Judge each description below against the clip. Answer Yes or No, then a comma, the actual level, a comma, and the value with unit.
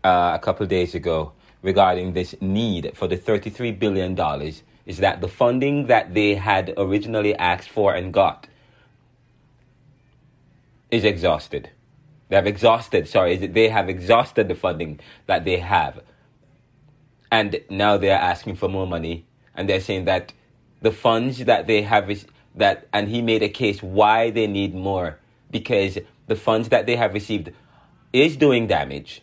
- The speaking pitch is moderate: No, low, 105 Hz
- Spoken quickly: No, average, 165 wpm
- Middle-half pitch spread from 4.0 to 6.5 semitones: Yes, average, 4.5 semitones